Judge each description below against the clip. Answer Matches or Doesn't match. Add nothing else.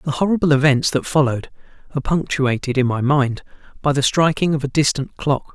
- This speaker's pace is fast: Doesn't match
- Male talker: Matches